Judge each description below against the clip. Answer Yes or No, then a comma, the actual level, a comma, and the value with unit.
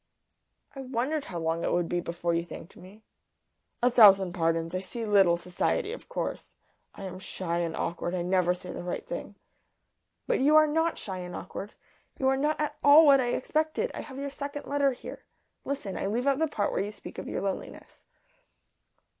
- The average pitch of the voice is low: No, high, 205 Hz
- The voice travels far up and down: Yes, wide, 7.9 semitones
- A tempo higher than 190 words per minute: Yes, average, 200 wpm